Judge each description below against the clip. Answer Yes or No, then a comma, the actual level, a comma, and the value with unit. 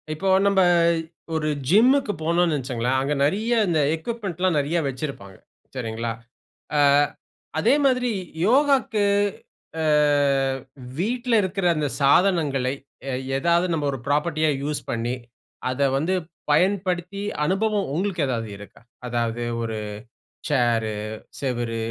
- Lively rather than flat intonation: Yes, wide, 7.1 semitones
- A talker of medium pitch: Yes, medium, 155 Hz